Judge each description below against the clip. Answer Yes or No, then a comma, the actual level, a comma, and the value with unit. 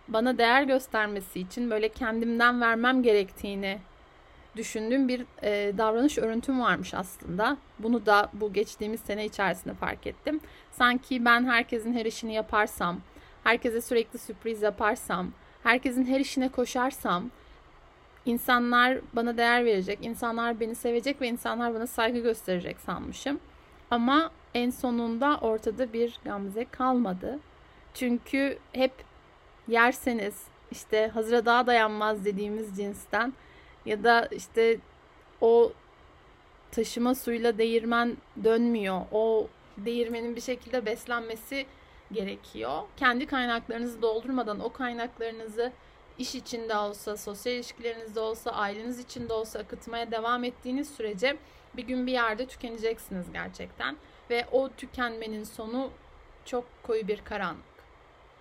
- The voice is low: No, high, 235 Hz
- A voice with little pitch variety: Yes, narrow, 2.1 semitones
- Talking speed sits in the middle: Yes, average, 115 wpm